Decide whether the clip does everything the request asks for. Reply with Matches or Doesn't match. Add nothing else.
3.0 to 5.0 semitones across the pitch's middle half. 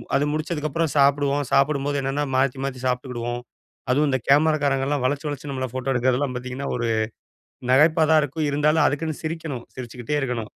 Doesn't match